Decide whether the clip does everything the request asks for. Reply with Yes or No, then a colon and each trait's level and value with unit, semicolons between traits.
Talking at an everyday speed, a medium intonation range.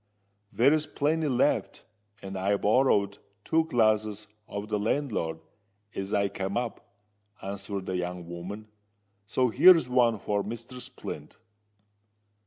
No: slow, 115 wpm; average, 4.1 semitones